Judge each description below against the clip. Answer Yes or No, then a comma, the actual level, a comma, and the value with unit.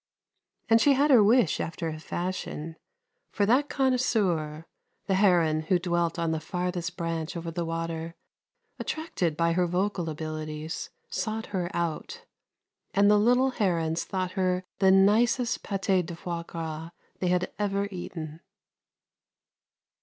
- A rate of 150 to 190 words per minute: No, average, 140 wpm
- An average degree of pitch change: Yes, average, 3.7 semitones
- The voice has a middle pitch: Yes, medium, 180 Hz